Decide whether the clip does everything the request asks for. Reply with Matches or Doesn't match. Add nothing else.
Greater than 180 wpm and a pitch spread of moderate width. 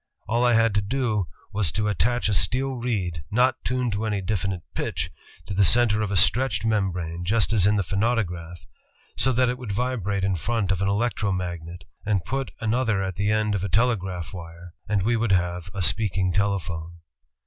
Matches